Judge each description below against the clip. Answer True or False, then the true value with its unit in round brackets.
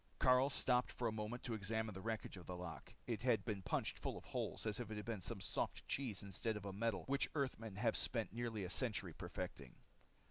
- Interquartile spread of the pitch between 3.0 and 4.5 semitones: True (3.3 semitones)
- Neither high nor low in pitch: False (110 Hz)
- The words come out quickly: True (225 wpm)